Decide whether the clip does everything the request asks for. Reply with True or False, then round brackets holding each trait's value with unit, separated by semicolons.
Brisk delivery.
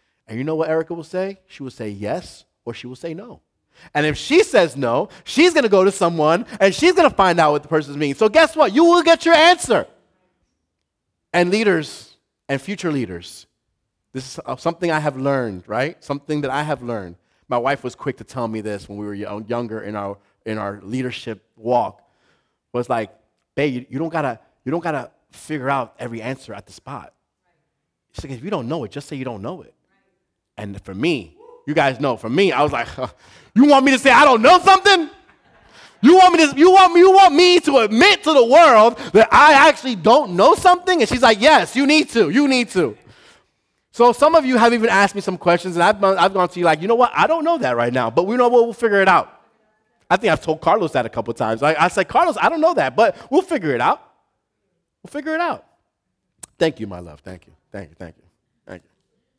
True (230 wpm)